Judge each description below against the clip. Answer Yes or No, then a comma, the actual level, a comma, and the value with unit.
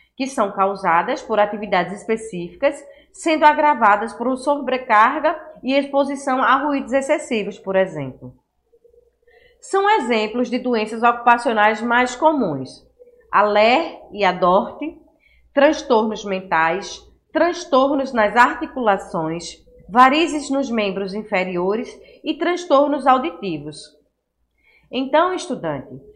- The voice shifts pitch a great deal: Yes, wide, 6.9 semitones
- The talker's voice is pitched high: Yes, very high, 250 Hz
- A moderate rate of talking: No, slow, 95 wpm